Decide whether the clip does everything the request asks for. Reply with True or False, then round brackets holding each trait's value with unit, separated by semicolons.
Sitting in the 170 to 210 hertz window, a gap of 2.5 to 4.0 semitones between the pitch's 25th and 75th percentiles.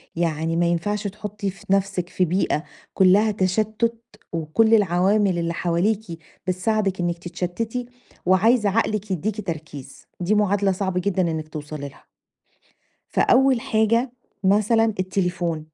True (190 Hz; 3.6 semitones)